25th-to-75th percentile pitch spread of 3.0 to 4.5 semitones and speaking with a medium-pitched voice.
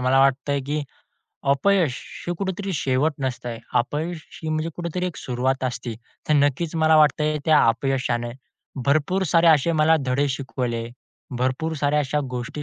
Yes: average, 3.6 semitones; medium, 145 Hz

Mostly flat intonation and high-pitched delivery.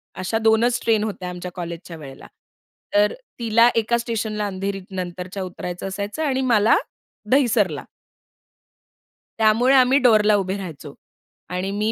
No: average, 3.8 semitones; high, 205 Hz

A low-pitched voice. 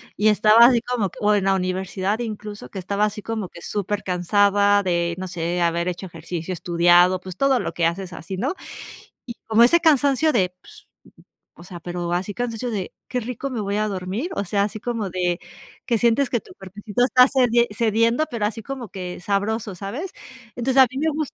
No: high, 205 Hz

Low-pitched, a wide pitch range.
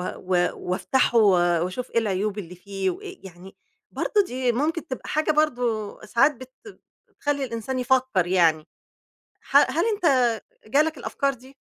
No: high, 235 Hz; wide, 6.2 semitones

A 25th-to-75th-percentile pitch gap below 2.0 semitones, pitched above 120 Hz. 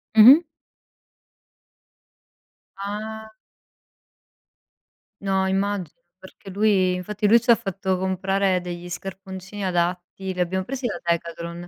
No: narrow, 2.3 semitones; high, 190 Hz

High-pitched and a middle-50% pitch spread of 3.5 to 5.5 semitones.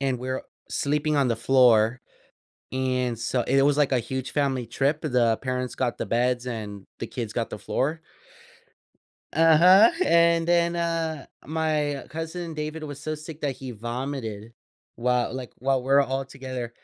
No: low, 135 Hz; average, 3.8 semitones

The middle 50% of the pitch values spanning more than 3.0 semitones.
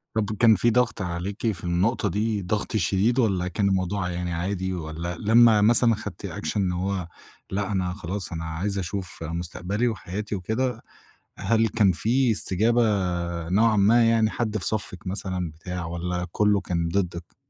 Yes: average, 3.6 semitones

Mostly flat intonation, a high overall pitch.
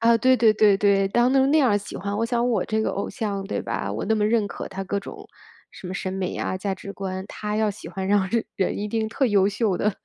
Yes: narrow, 2.3 semitones; high, 205 Hz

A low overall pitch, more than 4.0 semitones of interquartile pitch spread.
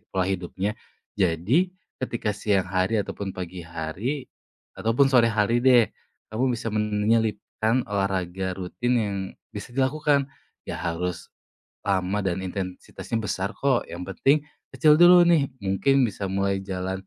Yes: low, 105 Hz; average, 4.8 semitones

